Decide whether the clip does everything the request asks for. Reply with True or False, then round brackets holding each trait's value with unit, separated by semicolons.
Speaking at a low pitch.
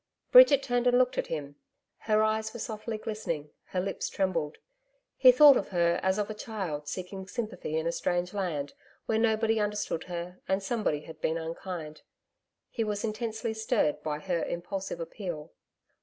False (195 Hz)